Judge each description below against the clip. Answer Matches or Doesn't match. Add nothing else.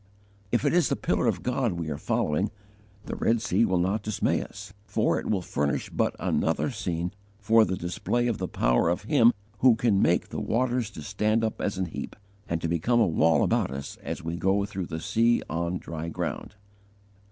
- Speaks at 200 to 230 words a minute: Matches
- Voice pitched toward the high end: Doesn't match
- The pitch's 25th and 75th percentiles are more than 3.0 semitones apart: Matches